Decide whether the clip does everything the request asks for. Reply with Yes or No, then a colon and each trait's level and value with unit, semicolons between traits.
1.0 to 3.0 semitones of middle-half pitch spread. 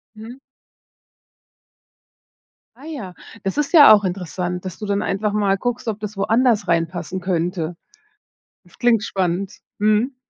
No: average, 3.8 semitones